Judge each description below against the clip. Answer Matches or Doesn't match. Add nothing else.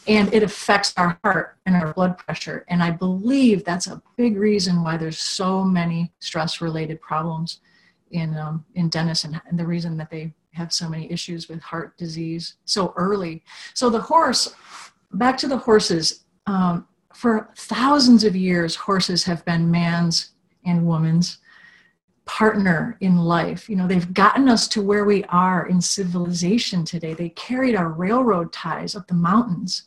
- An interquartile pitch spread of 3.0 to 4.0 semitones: Matches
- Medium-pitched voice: Matches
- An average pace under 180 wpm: Matches